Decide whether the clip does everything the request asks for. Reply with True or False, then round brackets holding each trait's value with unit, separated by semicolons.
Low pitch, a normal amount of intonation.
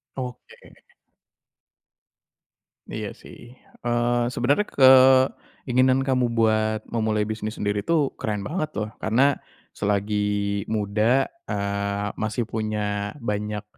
True (110 Hz; 3.7 semitones)